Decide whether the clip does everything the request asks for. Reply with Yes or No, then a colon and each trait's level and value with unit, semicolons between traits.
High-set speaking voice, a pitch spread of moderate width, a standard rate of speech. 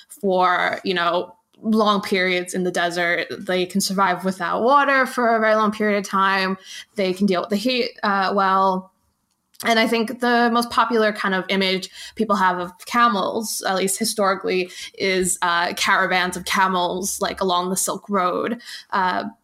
Yes: high, 195 Hz; average, 3.0 semitones; average, 170 wpm